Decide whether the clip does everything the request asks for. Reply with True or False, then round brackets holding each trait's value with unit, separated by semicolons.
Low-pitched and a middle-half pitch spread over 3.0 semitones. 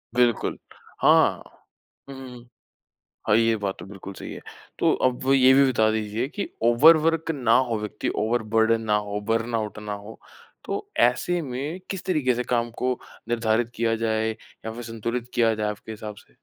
False (115 Hz; 2.5 semitones)